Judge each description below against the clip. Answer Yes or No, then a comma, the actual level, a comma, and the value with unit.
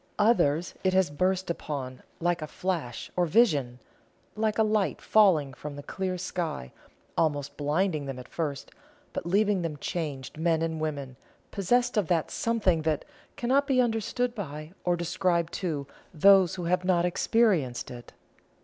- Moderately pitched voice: Yes, medium, 170 Hz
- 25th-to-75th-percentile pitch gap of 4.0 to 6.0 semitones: Yes, average, 4.8 semitones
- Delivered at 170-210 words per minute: No, average, 155 wpm